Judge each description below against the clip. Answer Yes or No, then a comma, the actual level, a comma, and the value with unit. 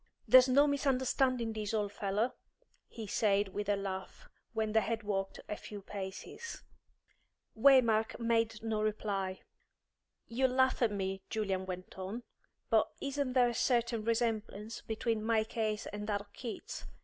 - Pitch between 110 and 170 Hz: No, high, 220 Hz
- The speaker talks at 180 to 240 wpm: No, average, 150 wpm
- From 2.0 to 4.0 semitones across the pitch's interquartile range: Yes, average, 2.8 semitones